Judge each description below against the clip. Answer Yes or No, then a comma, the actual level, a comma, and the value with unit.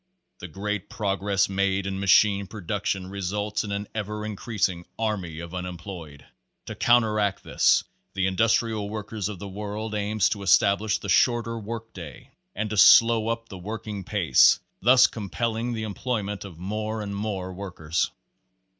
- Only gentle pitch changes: Yes, narrow, 2.2 semitones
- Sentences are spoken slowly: No, average, 155 wpm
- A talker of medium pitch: No, low, 100 Hz